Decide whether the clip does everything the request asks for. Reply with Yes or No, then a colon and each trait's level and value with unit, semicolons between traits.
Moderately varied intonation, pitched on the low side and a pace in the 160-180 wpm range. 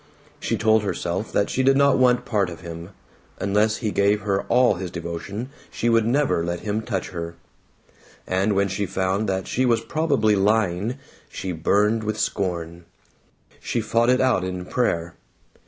Yes: average, 3.9 semitones; low, 100 Hz; average, 170 wpm